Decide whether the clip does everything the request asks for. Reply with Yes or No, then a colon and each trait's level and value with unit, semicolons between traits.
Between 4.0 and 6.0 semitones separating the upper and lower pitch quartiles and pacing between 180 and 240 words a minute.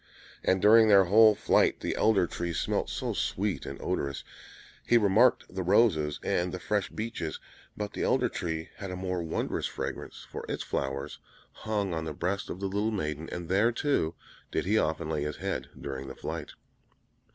Yes: average, 4.6 semitones; average, 185 wpm